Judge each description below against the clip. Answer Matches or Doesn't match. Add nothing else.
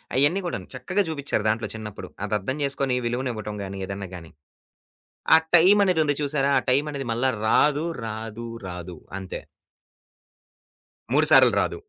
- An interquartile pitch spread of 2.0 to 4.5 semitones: Doesn't match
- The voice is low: Matches